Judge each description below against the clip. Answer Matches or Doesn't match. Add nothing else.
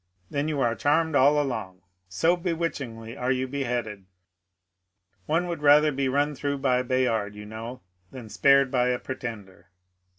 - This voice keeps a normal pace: Matches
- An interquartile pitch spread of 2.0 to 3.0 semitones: Doesn't match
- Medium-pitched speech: Doesn't match